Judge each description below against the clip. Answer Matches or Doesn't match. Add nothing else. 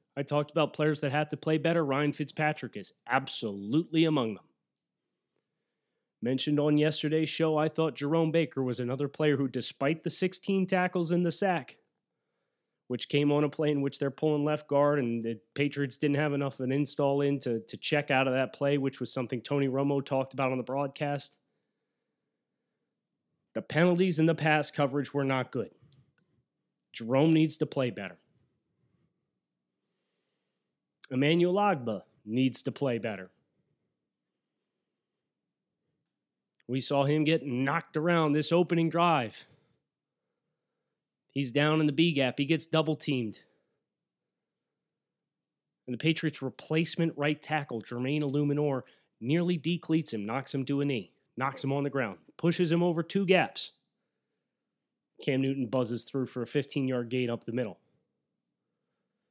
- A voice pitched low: Doesn't match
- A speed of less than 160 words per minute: Matches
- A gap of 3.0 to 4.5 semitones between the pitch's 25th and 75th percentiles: Matches